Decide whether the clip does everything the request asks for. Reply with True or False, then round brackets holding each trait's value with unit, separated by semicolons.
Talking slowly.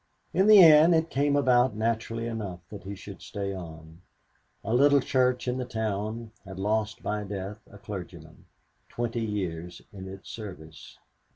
False (160 wpm)